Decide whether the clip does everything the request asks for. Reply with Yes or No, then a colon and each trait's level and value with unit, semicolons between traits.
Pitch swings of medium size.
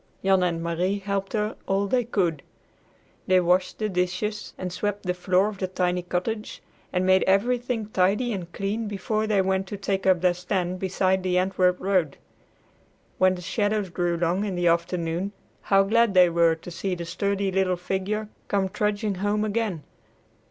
No: narrow, 2.3 semitones